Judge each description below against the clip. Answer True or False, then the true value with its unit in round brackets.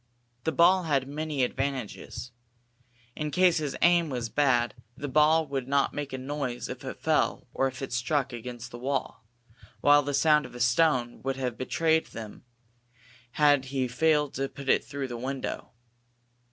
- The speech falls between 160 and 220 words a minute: True (170 wpm)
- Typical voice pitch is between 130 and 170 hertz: True (135 Hz)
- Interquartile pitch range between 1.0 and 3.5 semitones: True (2.9 semitones)